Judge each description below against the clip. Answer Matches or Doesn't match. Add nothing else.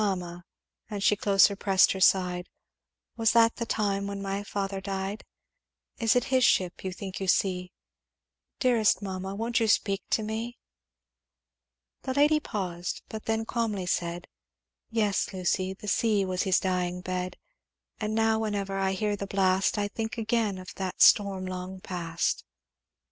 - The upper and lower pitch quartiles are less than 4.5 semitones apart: Matches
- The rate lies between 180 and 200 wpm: Doesn't match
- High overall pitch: Matches